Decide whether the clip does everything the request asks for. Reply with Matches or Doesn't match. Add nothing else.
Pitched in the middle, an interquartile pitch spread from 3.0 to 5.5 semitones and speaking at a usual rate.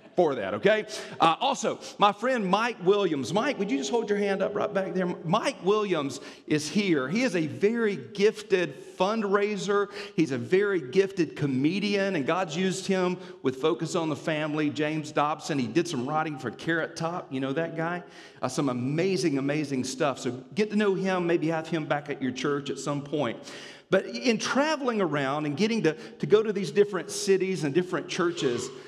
Matches